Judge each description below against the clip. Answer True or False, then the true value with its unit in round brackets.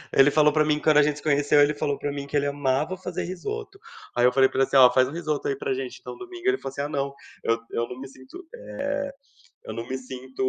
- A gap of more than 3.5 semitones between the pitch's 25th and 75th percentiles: False (2.6 semitones)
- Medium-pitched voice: True (145 Hz)